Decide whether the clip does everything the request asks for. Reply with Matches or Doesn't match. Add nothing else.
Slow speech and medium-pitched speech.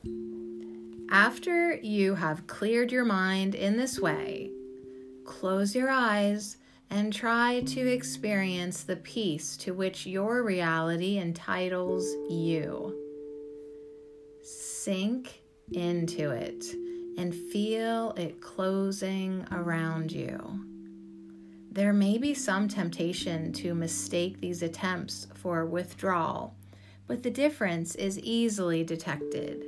Matches